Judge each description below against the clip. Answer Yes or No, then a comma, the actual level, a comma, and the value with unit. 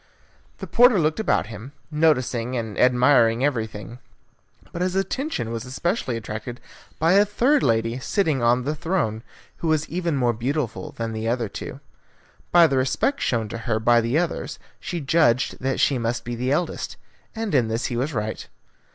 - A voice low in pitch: Yes, low, 130 Hz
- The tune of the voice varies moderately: No, wide, 5.8 semitones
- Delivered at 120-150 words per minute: No, average, 175 wpm